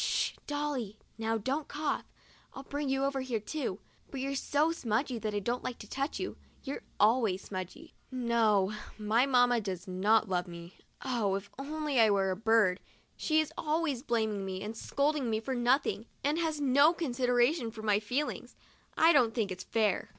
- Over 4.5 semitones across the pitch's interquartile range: Yes, average, 4.9 semitones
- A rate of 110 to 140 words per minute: No, average, 185 wpm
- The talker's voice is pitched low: No, high, 240 Hz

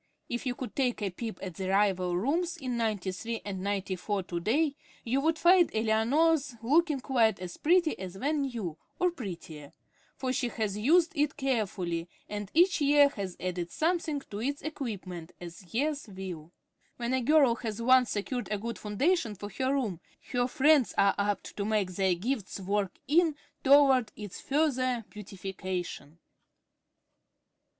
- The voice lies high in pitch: Yes, high, 230 Hz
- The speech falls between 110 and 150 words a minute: No, average, 160 wpm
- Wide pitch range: Yes, wide, 6.5 semitones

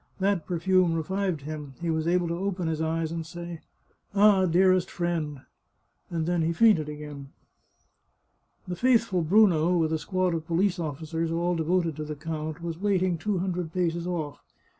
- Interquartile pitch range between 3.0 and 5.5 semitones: No, narrow, 2.5 semitones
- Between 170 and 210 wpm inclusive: Yes, average, 180 wpm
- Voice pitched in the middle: Yes, medium, 170 Hz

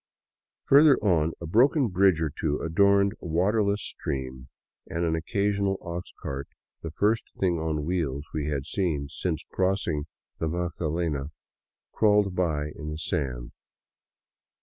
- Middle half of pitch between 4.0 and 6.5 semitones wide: Yes, average, 4.6 semitones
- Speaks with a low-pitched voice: Yes, very low, 85 Hz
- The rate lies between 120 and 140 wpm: Yes, slow, 135 wpm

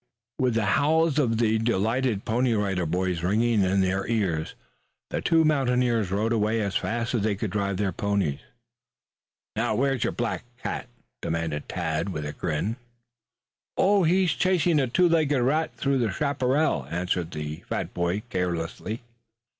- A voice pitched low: Yes, low, 110 Hz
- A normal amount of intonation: No, wide, 6.0 semitones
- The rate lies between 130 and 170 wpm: Yes, average, 155 wpm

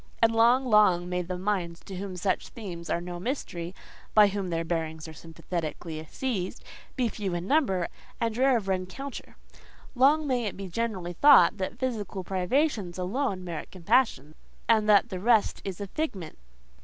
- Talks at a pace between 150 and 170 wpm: Yes, average, 160 wpm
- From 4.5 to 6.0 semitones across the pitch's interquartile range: Yes, average, 4.8 semitones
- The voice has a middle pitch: No, high, 195 Hz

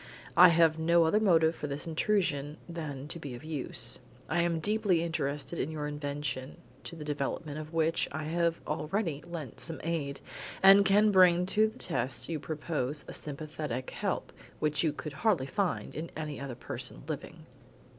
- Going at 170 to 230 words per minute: Yes, average, 175 wpm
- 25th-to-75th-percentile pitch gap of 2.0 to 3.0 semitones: Yes, average, 2.7 semitones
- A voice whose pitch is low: No, medium, 160 Hz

